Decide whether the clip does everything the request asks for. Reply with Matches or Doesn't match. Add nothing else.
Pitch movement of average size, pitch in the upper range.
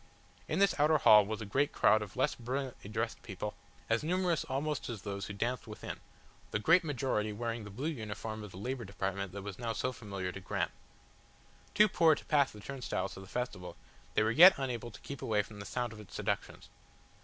Doesn't match